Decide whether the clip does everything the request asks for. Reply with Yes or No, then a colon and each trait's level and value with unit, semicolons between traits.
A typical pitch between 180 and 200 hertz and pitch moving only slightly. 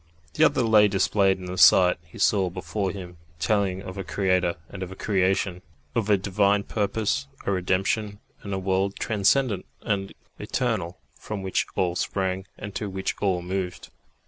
No: very low, 95 Hz; narrow, 1.7 semitones